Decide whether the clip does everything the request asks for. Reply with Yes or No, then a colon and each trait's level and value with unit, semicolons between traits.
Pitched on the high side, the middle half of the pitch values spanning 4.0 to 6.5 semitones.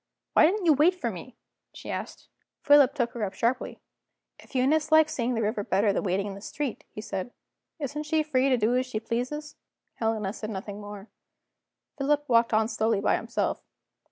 Yes: high, 240 Hz; wide, 5.5 semitones